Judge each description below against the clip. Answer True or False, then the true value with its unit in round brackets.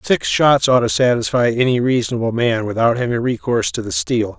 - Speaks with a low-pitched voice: True (120 Hz)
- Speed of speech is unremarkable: True (190 wpm)